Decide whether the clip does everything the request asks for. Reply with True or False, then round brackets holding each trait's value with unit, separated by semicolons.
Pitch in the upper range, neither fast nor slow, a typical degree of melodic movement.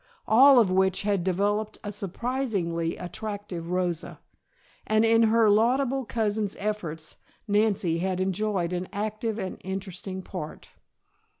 False (205 Hz; 120 wpm; 3.1 semitones)